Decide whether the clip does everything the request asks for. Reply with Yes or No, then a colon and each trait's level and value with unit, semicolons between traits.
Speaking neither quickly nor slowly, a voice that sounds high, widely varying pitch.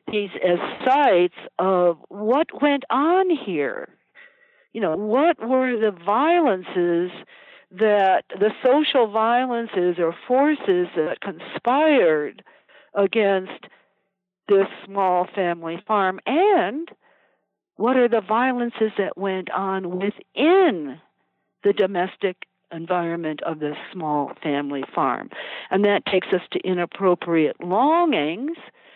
No: slow, 105 wpm; high, 205 Hz; wide, 7.0 semitones